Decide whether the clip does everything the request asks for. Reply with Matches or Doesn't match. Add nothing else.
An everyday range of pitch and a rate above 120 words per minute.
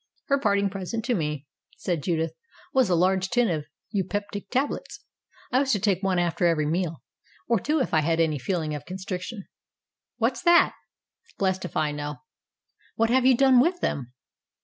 Doesn't match